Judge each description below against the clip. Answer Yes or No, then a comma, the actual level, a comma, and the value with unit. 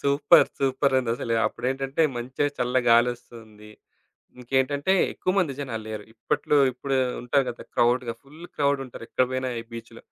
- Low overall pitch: Yes, low, 130 Hz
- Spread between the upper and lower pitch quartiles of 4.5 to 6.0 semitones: No, average, 2.8 semitones